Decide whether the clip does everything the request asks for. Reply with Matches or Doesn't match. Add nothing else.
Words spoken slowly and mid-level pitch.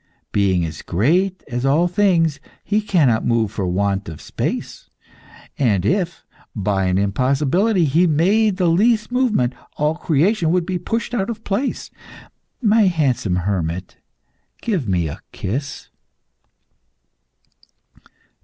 Matches